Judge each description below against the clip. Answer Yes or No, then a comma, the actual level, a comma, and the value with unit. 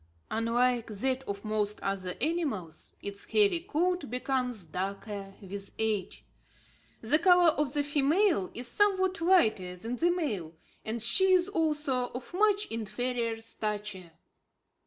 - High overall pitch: Yes, high, 245 Hz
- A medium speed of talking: No, slow, 130 wpm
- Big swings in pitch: Yes, wide, 8.1 semitones